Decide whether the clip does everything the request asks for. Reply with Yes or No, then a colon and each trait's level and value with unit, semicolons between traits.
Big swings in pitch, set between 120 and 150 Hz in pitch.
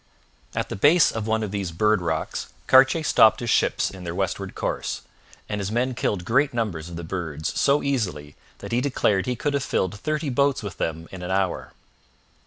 No: wide, 6.4 semitones; low, 105 Hz